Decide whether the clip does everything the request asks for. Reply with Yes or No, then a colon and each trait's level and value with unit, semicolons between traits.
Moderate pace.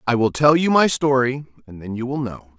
No: fast, 255 wpm